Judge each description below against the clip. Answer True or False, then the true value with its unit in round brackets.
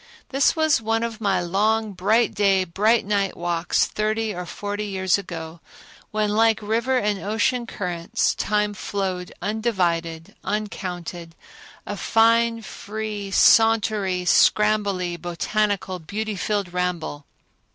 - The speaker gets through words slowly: True (120 wpm)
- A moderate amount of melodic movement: True (3.3 semitones)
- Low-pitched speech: False (205 Hz)